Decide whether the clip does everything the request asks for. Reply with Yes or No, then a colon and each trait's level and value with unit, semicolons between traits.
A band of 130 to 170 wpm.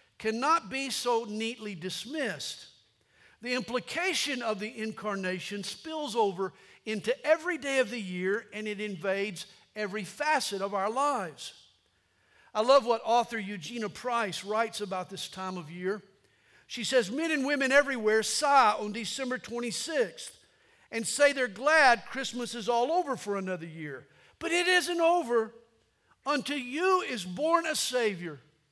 Yes: average, 145 wpm